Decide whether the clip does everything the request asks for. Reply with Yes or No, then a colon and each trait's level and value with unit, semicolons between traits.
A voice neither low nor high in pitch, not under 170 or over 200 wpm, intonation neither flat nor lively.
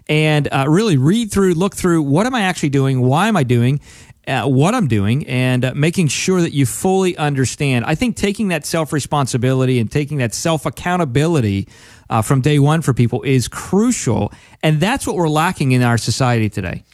Yes: medium, 145 Hz; average, 190 wpm; average, 5.0 semitones